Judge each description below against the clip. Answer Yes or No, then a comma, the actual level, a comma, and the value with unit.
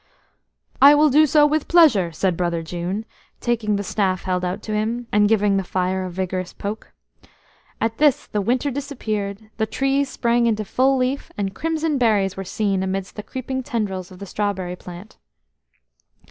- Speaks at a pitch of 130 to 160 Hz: No, high, 210 Hz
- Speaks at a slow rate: No, average, 175 wpm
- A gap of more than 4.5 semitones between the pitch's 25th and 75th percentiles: Yes, average, 5.3 semitones